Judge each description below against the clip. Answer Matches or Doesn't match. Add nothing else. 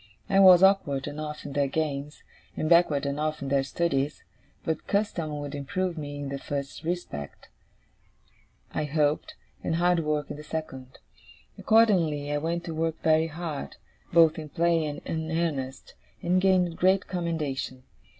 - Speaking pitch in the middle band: Matches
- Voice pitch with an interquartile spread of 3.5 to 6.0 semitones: Doesn't match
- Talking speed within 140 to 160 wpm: Matches